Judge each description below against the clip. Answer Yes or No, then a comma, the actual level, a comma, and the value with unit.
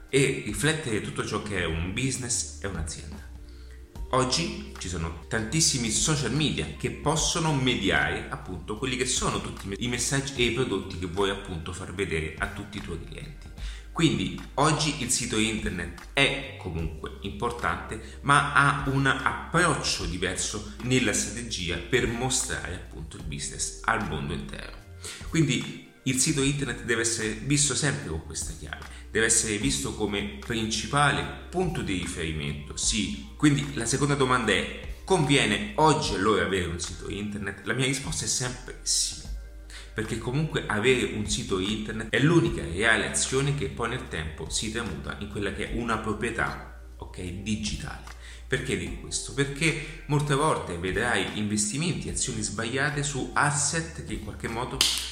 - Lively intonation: Yes, wide, 8.4 semitones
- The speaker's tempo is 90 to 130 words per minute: No, average, 150 wpm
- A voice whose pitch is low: Yes, low, 105 Hz